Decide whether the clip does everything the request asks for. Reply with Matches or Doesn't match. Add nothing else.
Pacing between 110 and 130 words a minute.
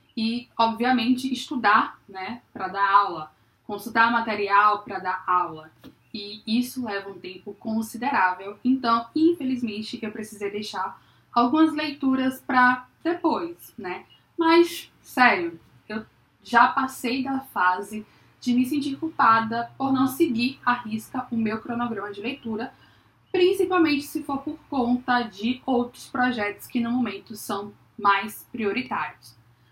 Matches